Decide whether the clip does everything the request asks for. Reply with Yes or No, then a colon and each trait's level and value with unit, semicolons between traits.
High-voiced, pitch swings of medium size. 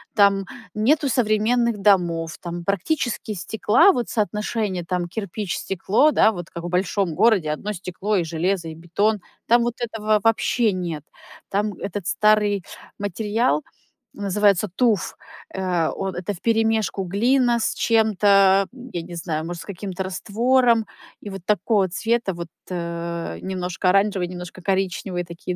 Yes: high, 200 Hz; average, 3.7 semitones